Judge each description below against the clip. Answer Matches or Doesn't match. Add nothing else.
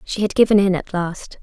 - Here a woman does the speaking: Matches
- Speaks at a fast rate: Matches